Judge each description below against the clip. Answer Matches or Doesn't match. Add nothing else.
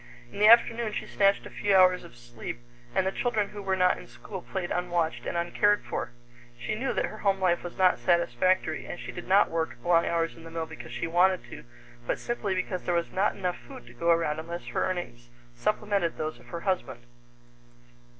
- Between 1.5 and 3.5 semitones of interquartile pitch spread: Matches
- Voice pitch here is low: Doesn't match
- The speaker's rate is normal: Doesn't match